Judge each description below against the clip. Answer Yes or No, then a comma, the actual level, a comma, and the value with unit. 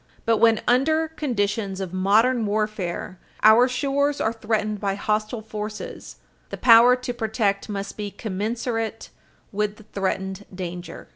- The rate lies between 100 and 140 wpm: Yes, slow, 135 wpm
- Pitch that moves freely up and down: No, average, 2.8 semitones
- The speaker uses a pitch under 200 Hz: No, high, 215 Hz